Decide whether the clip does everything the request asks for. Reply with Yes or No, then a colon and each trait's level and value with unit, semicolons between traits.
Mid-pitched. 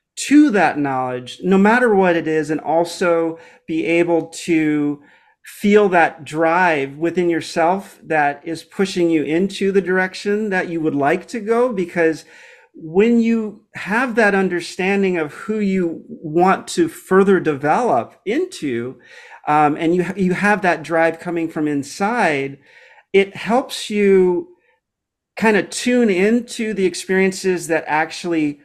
Yes: medium, 180 Hz